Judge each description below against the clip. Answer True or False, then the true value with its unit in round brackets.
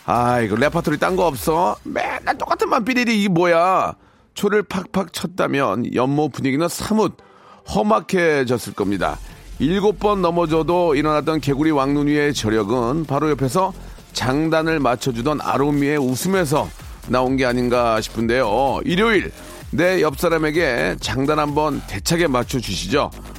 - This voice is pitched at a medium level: True (150 Hz)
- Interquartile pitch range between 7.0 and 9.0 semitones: False (5.3 semitones)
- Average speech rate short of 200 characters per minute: False (305 characters per minute)